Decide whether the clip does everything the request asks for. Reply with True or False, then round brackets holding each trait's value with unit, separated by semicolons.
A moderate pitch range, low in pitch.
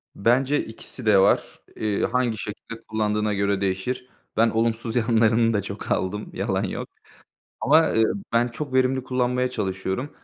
True (3.3 semitones; 115 Hz)